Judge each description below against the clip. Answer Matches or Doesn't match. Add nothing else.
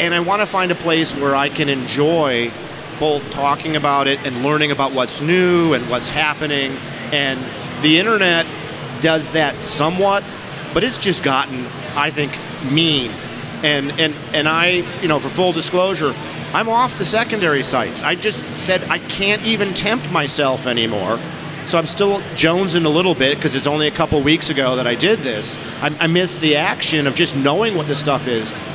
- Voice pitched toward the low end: Doesn't match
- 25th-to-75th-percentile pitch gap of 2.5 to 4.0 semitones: Matches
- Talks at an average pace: Matches